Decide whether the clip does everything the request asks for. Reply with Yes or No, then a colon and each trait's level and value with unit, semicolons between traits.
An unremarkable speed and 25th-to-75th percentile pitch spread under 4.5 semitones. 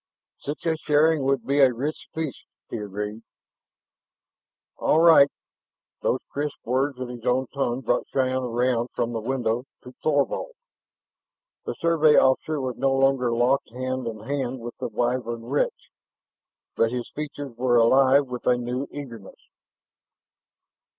Yes: average, 145 wpm; average, 2.7 semitones